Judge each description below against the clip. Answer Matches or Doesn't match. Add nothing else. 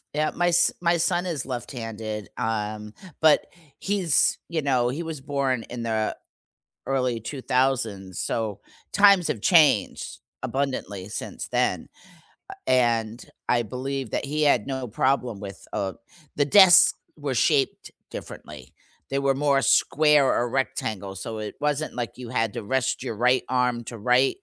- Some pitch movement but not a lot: Matches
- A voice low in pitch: Matches